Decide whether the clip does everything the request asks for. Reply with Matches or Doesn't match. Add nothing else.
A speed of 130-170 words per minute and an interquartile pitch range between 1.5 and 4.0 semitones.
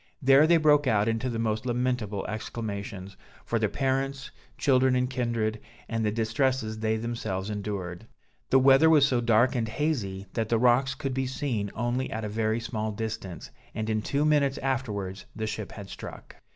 Doesn't match